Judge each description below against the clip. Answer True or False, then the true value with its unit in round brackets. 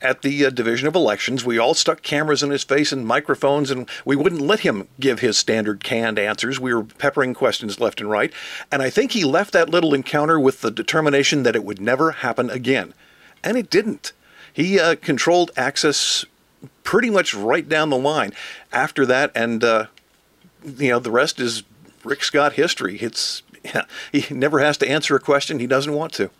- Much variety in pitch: False (3.7 semitones)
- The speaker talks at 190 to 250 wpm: True (200 wpm)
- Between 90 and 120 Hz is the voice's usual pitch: False (135 Hz)